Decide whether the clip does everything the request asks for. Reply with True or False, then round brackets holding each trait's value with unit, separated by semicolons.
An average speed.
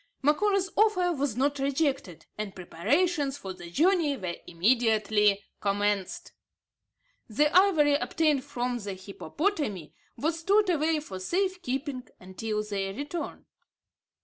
False (120 wpm)